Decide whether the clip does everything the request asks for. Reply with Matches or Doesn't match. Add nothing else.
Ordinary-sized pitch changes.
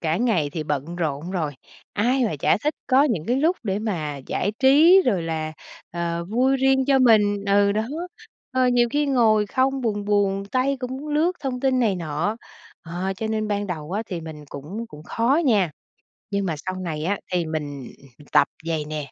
Doesn't match